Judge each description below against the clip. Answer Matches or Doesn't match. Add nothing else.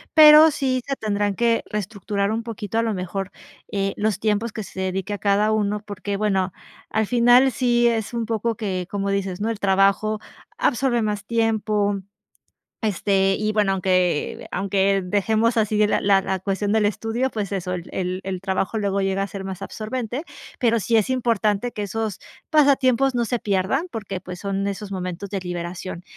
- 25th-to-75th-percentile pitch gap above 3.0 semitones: Doesn't match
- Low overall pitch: Doesn't match